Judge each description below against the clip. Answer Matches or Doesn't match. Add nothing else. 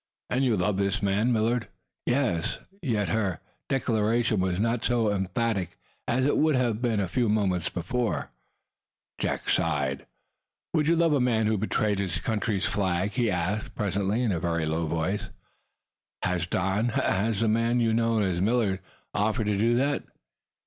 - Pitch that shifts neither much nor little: Matches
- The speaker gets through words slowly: Doesn't match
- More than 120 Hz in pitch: Doesn't match